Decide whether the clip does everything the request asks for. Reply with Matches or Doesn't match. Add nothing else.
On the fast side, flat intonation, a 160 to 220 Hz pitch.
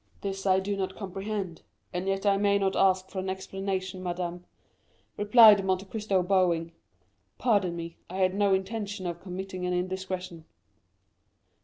Doesn't match